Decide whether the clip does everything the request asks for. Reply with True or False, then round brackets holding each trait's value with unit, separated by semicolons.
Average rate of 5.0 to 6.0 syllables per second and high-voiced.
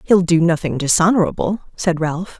False (5.1 syllables/s; 170 Hz)